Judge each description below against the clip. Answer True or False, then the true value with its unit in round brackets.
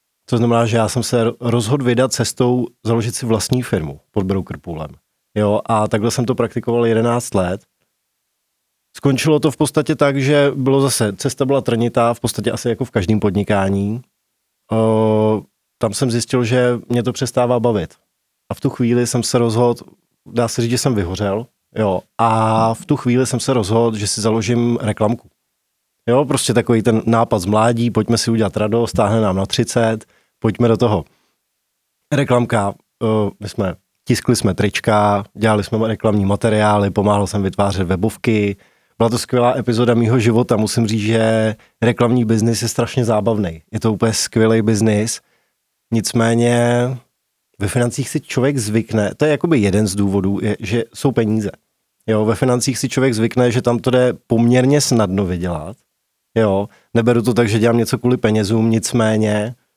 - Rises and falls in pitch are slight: True (2.3 semitones)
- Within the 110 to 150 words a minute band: False (170 wpm)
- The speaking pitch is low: True (115 Hz)